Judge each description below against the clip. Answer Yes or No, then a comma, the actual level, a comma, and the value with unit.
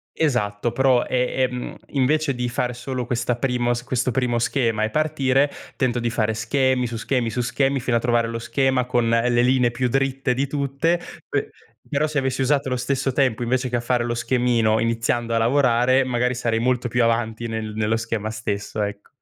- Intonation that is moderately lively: No, narrow, 2.2 semitones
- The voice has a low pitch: Yes, low, 125 Hz